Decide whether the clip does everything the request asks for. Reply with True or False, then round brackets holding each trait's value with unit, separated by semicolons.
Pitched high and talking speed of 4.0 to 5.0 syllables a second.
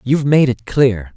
False (125 Hz; 4.8 syllables/s)